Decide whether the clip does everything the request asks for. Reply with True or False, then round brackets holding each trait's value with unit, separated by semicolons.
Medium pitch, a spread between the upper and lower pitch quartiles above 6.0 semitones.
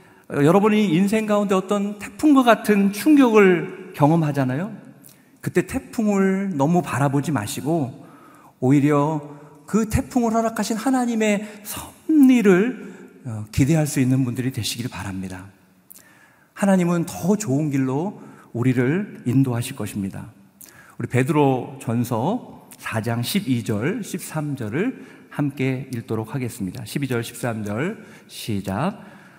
True (150 Hz; 8.2 semitones)